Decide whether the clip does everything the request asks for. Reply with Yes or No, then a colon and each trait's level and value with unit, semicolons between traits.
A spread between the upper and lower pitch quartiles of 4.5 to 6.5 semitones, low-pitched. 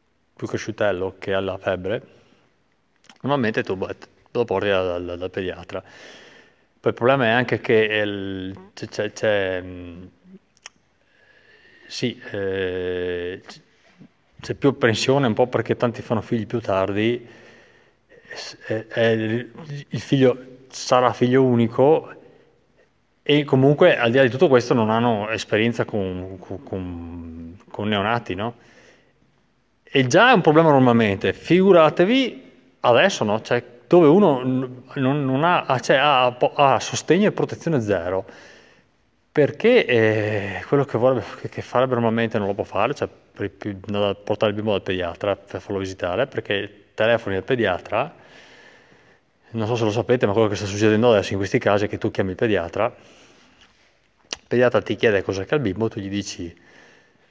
Yes: average, 4.8 semitones; low, 115 Hz